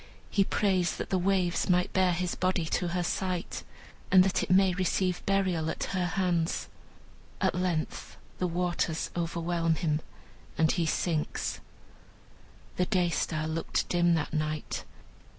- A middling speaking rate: Yes, average, 145 wpm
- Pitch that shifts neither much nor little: No, narrow, 1.8 semitones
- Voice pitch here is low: No, medium, 175 Hz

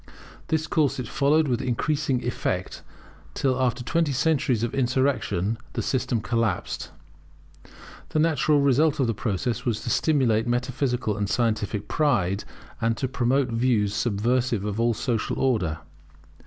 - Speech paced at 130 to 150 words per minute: Yes, average, 140 wpm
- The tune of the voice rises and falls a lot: No, average, 3.7 semitones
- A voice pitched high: No, low, 125 Hz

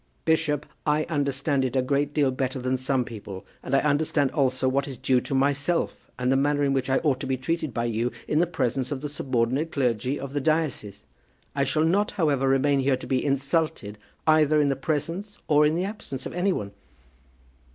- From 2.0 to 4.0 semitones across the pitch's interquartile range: Yes, average, 2.7 semitones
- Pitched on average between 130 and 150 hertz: Yes, medium, 140 Hz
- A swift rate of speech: Yes, fast, 210 wpm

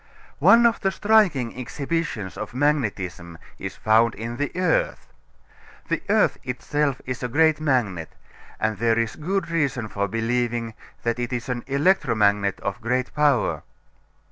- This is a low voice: Yes, low, 125 Hz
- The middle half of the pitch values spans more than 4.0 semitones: Yes, average, 4.9 semitones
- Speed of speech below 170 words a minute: Yes, average, 140 wpm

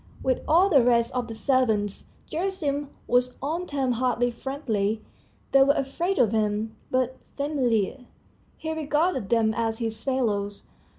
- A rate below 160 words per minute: Yes, average, 140 wpm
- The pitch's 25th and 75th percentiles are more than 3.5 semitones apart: Yes, average, 4.1 semitones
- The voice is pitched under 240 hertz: No, very high, 250 Hz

